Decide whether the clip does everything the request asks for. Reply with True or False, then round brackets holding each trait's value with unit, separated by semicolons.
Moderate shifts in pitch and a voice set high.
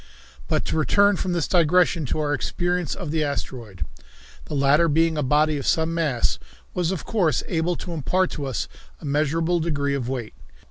False (3.4 semitones; 155 Hz)